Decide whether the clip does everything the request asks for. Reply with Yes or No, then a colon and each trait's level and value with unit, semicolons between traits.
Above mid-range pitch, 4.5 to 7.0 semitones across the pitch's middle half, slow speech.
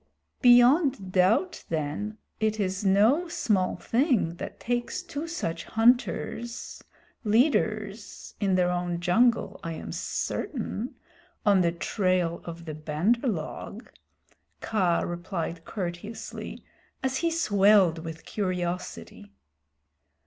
Yes: high, 200 Hz; wide, 5.5 semitones; slow, 105 wpm